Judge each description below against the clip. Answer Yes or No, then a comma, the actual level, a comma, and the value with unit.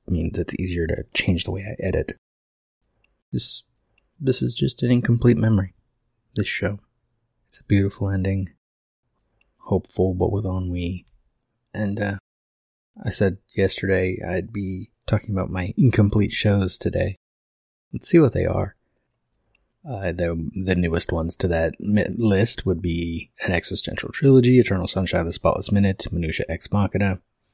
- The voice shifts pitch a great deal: No, average, 3.2 semitones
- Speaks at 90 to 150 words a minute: Yes, average, 145 wpm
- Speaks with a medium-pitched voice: No, very low, 95 Hz